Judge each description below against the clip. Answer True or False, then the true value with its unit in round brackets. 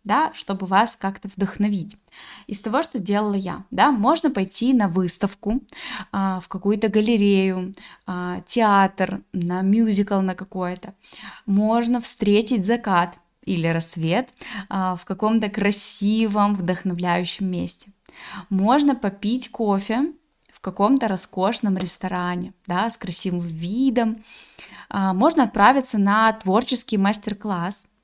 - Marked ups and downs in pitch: False (3.0 semitones)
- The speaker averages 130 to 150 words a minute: False (115 wpm)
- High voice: True (205 Hz)